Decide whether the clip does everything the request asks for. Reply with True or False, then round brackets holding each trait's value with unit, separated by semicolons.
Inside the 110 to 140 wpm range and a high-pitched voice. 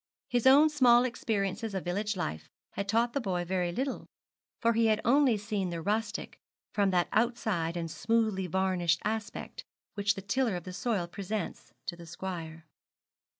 False (165 wpm; 200 Hz)